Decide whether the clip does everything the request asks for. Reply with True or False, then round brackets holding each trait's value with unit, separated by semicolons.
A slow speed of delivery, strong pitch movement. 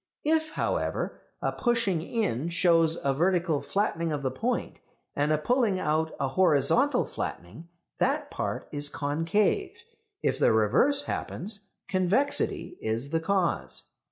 True (130 wpm; 6.7 semitones)